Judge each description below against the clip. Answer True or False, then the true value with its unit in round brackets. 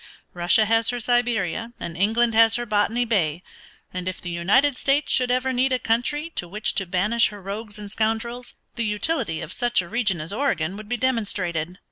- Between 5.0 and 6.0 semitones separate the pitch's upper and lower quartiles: False (4.6 semitones)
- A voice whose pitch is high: True (220 Hz)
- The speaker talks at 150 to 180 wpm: False (195 wpm)